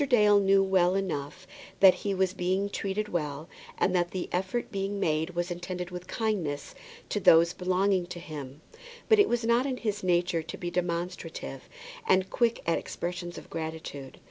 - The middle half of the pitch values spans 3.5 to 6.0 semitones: No, narrow, 2.4 semitones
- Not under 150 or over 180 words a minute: Yes, average, 170 wpm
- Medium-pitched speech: Yes, medium, 180 Hz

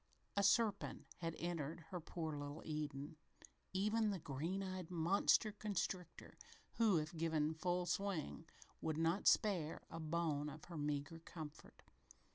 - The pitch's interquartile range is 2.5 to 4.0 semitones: Yes, average, 3.5 semitones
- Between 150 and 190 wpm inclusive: No, slow, 135 wpm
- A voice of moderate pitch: Yes, medium, 165 Hz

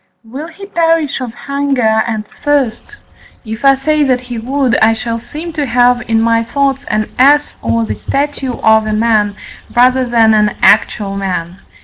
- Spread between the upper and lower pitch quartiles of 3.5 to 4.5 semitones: Yes, average, 4.2 semitones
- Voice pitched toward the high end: Yes, high, 245 Hz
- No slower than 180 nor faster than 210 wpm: No, average, 170 wpm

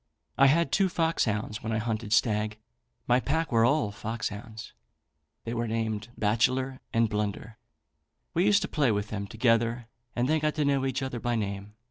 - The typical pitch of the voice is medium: No, low, 115 Hz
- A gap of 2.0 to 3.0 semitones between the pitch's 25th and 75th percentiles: No, average, 3.9 semitones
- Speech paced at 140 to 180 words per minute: Yes, average, 175 wpm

